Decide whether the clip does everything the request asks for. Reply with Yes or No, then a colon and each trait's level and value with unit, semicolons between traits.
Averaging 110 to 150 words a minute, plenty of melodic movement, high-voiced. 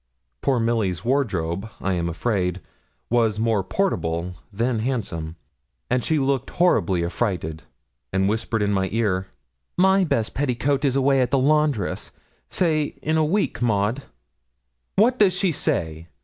No: average, 140 wpm; wide, 6.9 semitones; low, 115 Hz